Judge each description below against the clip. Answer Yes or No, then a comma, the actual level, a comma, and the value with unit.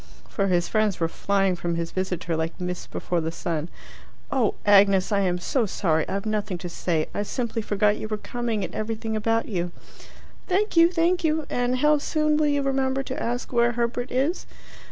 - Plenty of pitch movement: Yes, wide, 6.2 semitones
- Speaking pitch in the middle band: No, high, 215 Hz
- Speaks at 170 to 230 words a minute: Yes, average, 195 wpm